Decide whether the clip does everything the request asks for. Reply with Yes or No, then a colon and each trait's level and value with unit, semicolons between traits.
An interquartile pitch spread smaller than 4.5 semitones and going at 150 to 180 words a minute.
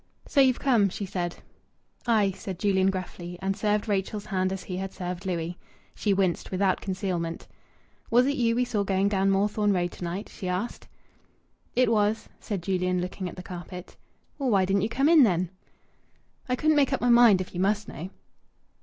No: average, 2.8 semitones; average, 190 wpm